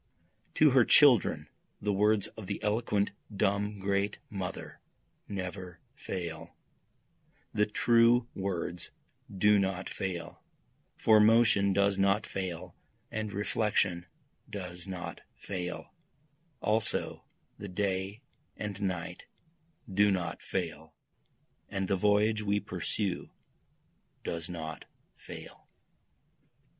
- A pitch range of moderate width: No, narrow, 2.3 semitones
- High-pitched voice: No, low, 100 Hz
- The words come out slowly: Yes, slow, 100 wpm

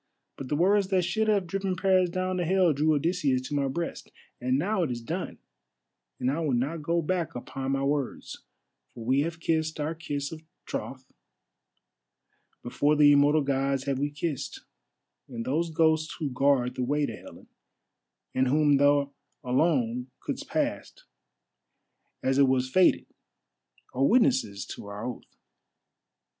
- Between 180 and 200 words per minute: No, average, 155 wpm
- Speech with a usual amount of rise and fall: Yes, average, 4.1 semitones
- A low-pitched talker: No, medium, 145 Hz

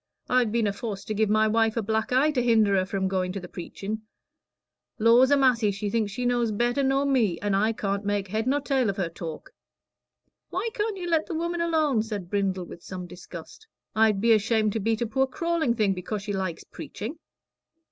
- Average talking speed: No, fast, 210 wpm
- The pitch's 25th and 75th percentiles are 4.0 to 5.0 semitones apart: Yes, average, 4.3 semitones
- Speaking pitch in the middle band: No, high, 220 Hz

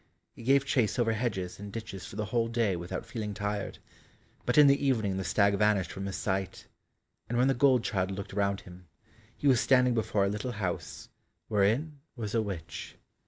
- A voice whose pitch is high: No, low, 105 Hz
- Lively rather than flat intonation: No, average, 3.8 semitones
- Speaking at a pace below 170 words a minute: No, average, 195 wpm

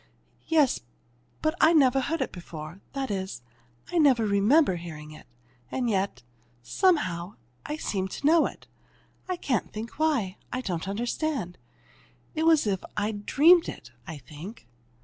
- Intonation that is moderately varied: No, wide, 8.7 semitones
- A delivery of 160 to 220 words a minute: No, average, 150 wpm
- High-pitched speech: Yes, high, 220 Hz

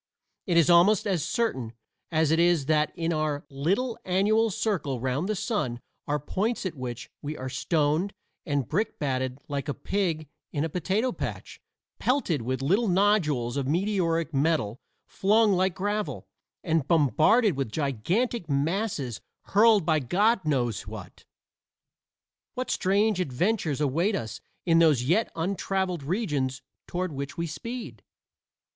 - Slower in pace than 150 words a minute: Yes, average, 140 wpm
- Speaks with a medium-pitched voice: Yes, medium, 165 Hz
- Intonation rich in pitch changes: Yes, wide, 6.2 semitones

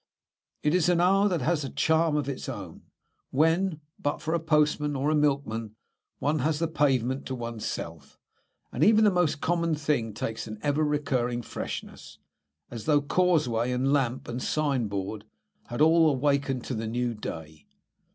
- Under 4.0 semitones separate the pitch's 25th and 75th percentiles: No, average, 4.7 semitones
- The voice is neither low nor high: Yes, medium, 145 Hz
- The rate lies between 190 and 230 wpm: No, average, 165 wpm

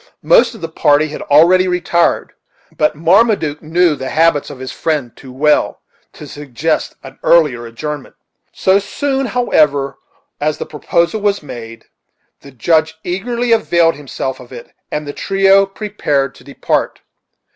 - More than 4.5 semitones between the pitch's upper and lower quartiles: Yes, average, 5.0 semitones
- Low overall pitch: No, medium, 155 Hz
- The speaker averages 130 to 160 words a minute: Yes, average, 145 wpm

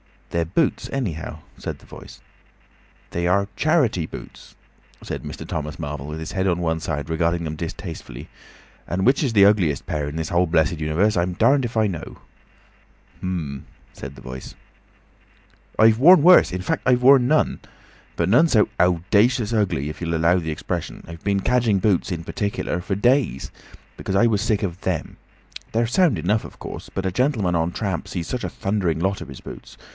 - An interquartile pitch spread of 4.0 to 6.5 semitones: Yes, wide, 5.4 semitones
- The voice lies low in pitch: Yes, very low, 95 Hz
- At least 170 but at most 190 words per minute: Yes, average, 175 wpm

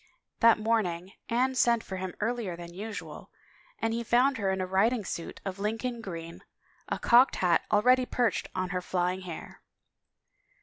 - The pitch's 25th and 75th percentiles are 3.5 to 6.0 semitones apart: Yes, average, 4.3 semitones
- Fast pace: No, average, 165 wpm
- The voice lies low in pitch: No, high, 210 Hz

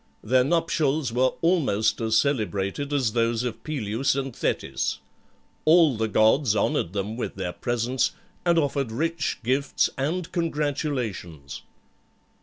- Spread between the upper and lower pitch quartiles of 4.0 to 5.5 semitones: Yes, average, 5.0 semitones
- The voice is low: Yes, low, 130 Hz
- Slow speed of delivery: Yes, slow, 125 wpm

